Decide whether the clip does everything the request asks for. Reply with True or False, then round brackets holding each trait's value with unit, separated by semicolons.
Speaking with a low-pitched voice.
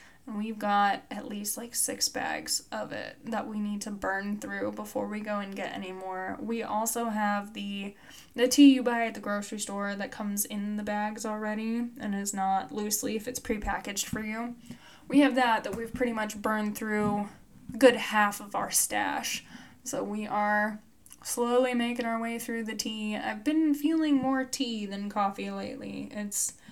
False (215 Hz)